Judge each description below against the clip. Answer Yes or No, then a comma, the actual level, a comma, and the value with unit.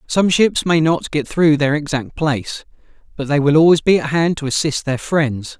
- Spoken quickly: Yes, fast, 215 wpm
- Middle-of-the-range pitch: Yes, medium, 150 Hz